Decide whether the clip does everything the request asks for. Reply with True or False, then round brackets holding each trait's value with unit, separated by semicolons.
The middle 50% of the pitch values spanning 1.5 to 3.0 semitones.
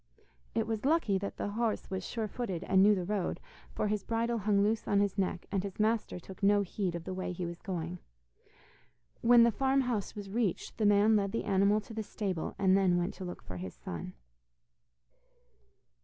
True (2.7 semitones)